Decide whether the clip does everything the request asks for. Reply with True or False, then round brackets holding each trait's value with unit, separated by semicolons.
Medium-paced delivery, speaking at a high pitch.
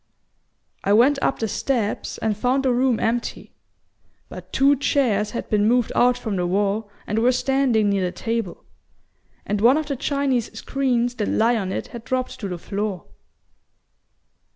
True (170 wpm; 235 Hz)